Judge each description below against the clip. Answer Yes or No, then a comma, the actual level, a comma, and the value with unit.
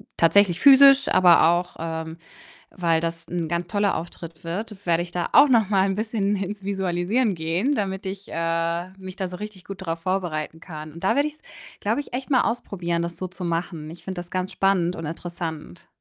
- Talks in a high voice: No, medium, 180 Hz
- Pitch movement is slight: No, average, 3.1 semitones